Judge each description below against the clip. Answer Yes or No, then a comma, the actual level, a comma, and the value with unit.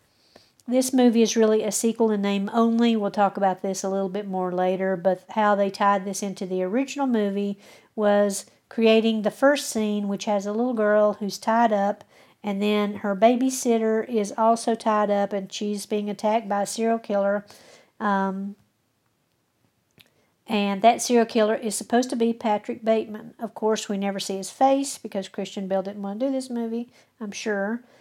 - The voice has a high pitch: Yes, high, 210 Hz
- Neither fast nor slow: Yes, average, 180 wpm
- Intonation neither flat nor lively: No, narrow, 2.3 semitones